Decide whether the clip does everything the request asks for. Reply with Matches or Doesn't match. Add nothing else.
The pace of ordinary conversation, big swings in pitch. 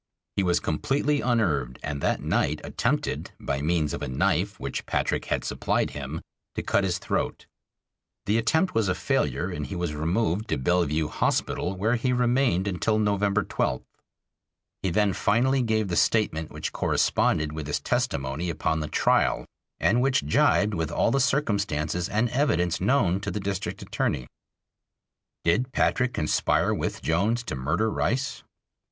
Matches